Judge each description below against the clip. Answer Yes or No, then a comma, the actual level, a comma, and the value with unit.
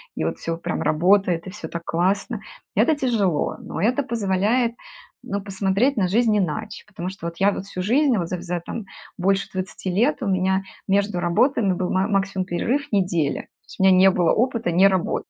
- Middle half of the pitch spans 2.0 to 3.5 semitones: Yes, average, 3.0 semitones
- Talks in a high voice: Yes, high, 195 Hz